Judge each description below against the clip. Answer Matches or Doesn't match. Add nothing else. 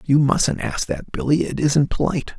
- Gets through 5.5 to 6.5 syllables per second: Doesn't match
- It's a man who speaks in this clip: Matches